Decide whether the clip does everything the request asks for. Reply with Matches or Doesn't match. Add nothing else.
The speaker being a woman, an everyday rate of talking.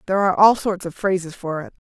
Doesn't match